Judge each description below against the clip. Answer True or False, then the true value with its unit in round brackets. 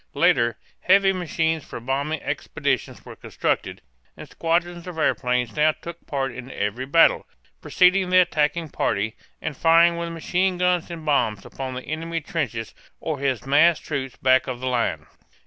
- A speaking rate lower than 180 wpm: True (160 wpm)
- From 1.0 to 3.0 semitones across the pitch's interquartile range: False (4.7 semitones)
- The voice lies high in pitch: False (155 Hz)